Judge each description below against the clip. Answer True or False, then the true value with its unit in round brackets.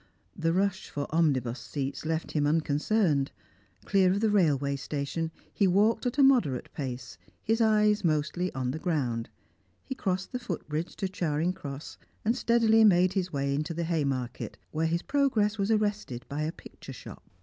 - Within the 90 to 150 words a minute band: False (170 wpm)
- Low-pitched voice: False (165 Hz)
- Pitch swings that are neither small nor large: False (6.4 semitones)